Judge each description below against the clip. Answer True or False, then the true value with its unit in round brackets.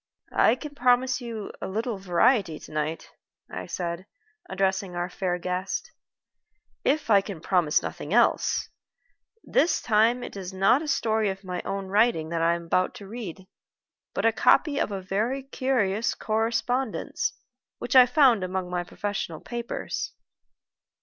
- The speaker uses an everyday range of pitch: True (4.9 semitones)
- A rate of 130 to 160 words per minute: True (150 wpm)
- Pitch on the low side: False (200 Hz)